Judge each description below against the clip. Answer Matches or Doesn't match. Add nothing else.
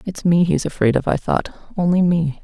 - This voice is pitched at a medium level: Matches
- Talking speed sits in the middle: Doesn't match